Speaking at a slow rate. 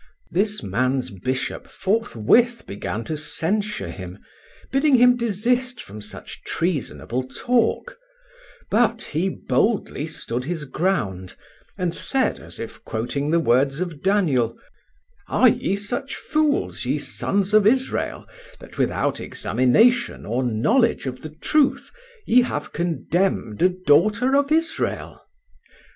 Yes: slow, 125 wpm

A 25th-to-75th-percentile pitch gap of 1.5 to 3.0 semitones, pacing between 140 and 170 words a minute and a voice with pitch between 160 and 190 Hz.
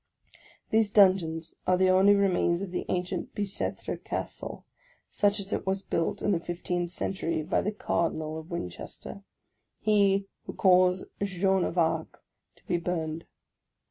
Yes: average, 2.7 semitones; average, 150 wpm; medium, 185 Hz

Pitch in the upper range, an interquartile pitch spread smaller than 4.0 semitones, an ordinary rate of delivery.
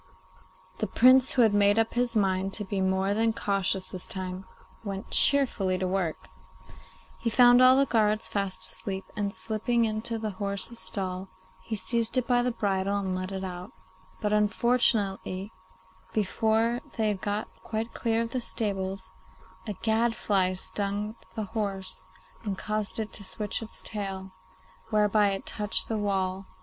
Yes: high, 205 Hz; average, 2.8 semitones; average, 160 wpm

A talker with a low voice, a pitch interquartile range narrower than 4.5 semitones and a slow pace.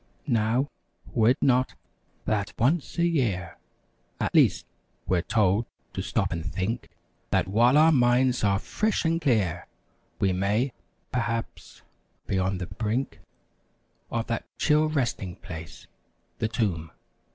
No: low, 115 Hz; average, 5.1 semitones; slow, 130 wpm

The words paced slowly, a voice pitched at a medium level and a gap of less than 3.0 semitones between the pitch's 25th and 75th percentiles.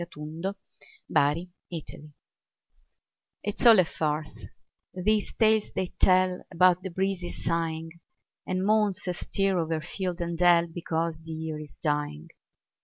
Yes: slow, 120 wpm; medium, 175 Hz; narrow, 2.6 semitones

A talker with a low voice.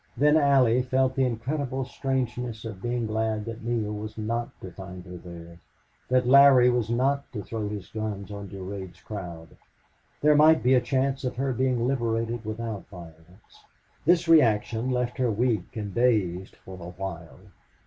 Yes: low, 115 Hz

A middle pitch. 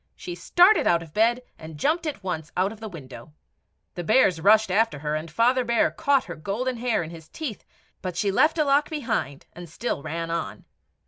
No: high, 200 Hz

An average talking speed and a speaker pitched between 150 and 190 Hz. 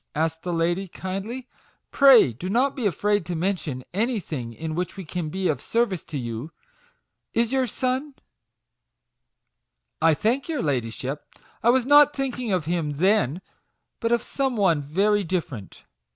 Yes: average, 160 wpm; medium, 185 Hz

